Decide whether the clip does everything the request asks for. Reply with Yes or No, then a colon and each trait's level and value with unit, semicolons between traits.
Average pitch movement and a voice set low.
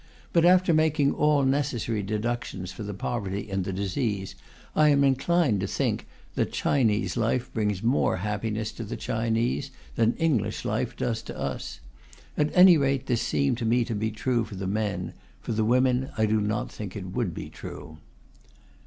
Yes: average, 4.5 semitones; low, 115 Hz